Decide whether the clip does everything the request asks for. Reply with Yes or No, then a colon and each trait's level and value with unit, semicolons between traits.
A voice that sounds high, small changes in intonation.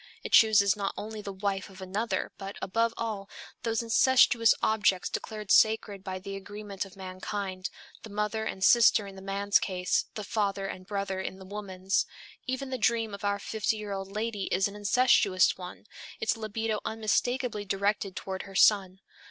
Yes: high, 200 Hz; narrow, 2.1 semitones